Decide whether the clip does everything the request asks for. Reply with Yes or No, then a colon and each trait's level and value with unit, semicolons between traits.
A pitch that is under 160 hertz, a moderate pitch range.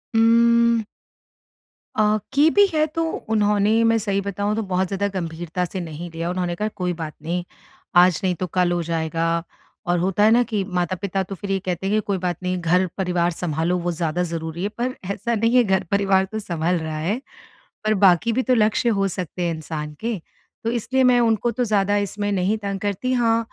No: high, 195 Hz; average, 3.9 semitones